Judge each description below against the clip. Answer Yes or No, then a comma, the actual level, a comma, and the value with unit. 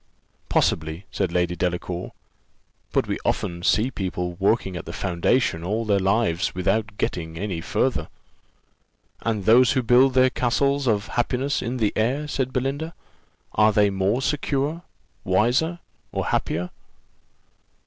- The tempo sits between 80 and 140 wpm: Yes, slow, 135 wpm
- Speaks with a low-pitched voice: Yes, low, 110 Hz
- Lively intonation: Yes, wide, 5.9 semitones